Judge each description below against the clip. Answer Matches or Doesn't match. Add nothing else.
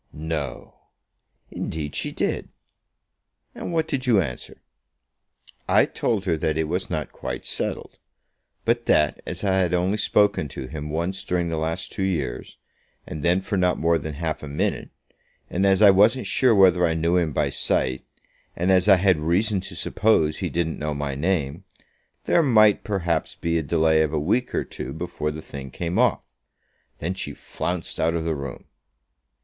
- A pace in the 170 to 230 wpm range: Matches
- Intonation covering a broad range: Doesn't match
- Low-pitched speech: Matches